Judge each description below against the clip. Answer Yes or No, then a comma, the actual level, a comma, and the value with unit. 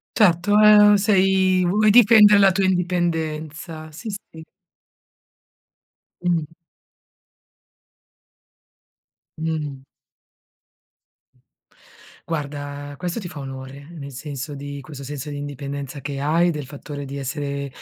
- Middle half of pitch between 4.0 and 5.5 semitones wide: Yes, average, 4.6 semitones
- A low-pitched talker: No, medium, 155 Hz